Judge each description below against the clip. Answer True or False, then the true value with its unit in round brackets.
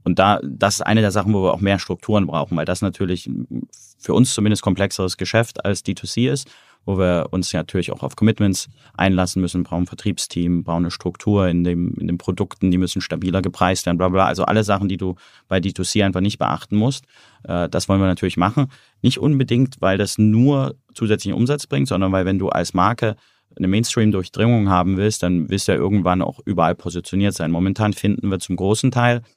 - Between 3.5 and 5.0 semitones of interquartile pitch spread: False (3.0 semitones)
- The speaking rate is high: True (205 wpm)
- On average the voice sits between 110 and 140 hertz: False (95 Hz)